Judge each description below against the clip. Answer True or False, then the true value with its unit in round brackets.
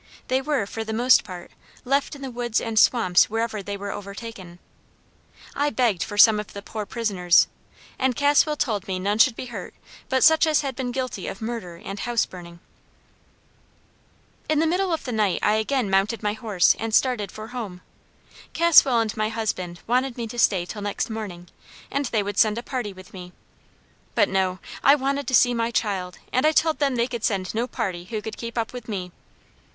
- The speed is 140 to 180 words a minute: False (200 wpm)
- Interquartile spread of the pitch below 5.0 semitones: True (4.1 semitones)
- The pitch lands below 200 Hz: False (225 Hz)